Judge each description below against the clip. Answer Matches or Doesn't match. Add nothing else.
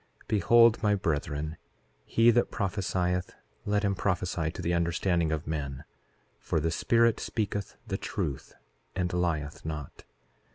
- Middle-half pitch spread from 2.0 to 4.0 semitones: Doesn't match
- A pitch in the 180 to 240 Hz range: Doesn't match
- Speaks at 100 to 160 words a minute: Matches